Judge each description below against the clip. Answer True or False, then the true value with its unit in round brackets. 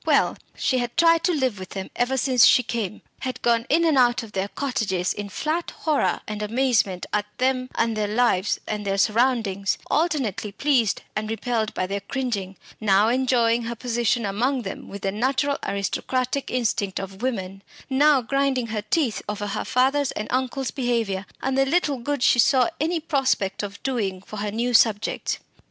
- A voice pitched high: True (235 Hz)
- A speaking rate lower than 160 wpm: False (180 wpm)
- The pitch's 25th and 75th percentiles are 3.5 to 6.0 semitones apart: True (4.3 semitones)